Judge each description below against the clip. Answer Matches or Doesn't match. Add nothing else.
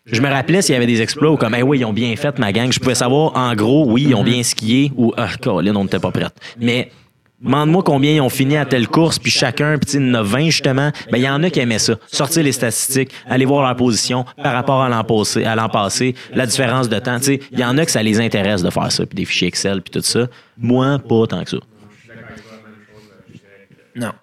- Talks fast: Matches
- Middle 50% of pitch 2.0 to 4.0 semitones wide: Matches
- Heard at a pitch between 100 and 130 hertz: Matches